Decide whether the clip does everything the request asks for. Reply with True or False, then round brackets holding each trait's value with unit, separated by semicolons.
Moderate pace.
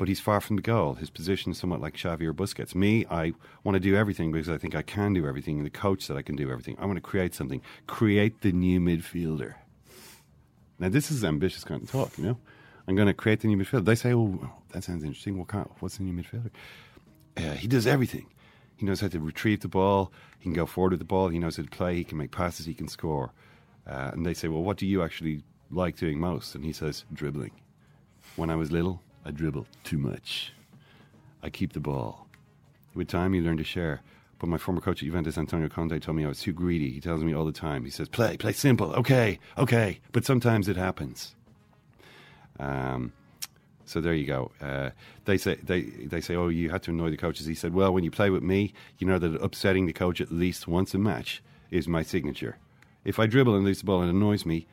False (240 wpm)